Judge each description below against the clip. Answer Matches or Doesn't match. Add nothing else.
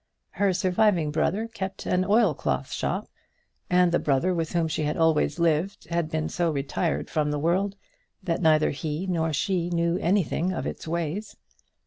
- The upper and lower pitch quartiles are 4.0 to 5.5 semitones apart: Doesn't match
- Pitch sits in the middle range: Matches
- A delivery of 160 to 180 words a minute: Matches